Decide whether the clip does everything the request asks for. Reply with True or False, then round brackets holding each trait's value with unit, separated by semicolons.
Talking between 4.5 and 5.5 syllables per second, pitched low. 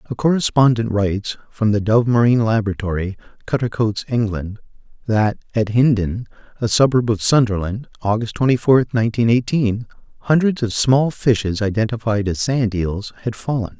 True (5.2 syllables/s; 115 Hz)